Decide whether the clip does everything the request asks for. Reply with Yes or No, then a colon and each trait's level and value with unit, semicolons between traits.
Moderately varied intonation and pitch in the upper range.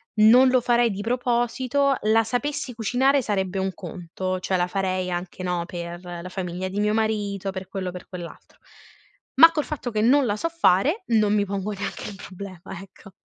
Yes: average, 4.6 semitones; high, 205 Hz